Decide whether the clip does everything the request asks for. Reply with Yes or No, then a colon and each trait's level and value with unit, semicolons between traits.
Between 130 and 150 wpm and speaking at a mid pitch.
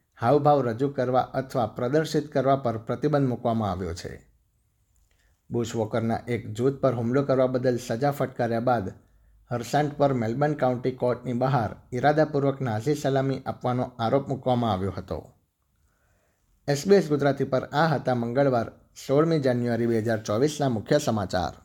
No: average, 135 wpm; low, 125 Hz